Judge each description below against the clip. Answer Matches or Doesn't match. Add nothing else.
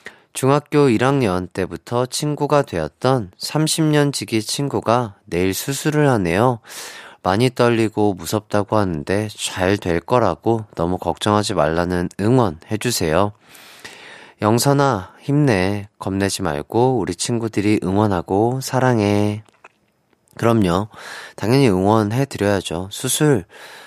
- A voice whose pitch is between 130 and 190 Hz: Doesn't match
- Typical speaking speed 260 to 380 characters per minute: Doesn't match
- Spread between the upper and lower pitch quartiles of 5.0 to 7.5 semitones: Matches